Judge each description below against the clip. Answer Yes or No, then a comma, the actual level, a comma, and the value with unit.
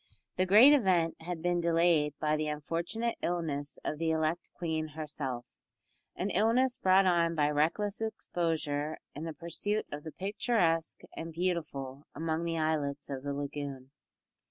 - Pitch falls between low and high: Yes, medium, 165 Hz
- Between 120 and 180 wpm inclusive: Yes, average, 150 wpm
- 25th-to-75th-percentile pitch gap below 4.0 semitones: Yes, average, 3.1 semitones